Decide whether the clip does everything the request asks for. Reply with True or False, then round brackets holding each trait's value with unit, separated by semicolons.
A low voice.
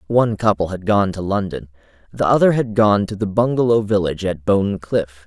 True (100 Hz)